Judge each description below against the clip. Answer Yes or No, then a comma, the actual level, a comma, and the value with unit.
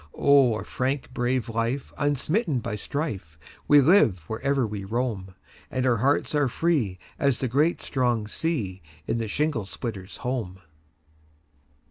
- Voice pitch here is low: Yes, low, 120 Hz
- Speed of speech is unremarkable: No, slow, 120 wpm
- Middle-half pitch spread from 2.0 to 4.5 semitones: No, average, 5.3 semitones